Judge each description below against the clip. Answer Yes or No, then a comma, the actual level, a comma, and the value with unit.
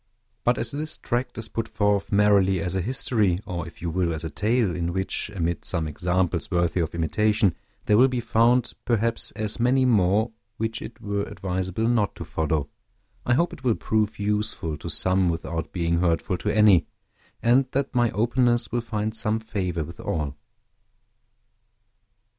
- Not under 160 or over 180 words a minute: Yes, average, 170 wpm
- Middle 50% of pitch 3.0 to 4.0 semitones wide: No, average, 5.0 semitones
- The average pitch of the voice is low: Yes, low, 105 Hz